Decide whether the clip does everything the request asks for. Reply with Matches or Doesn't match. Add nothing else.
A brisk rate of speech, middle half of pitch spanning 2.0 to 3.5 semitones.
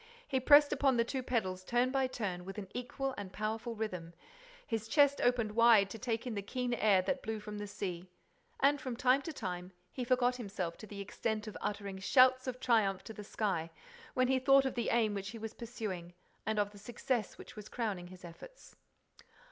Doesn't match